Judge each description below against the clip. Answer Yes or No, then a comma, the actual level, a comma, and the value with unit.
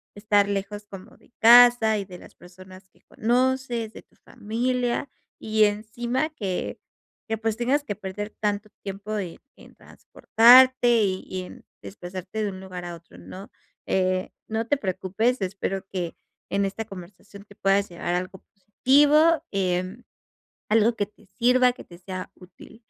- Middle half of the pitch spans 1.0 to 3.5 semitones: No, average, 3.9 semitones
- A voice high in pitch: Yes, high, 205 Hz